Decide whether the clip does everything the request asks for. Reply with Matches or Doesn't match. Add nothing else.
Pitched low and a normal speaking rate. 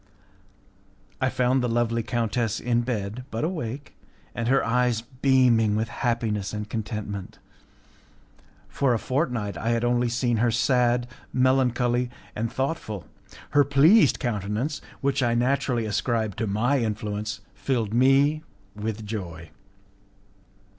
Doesn't match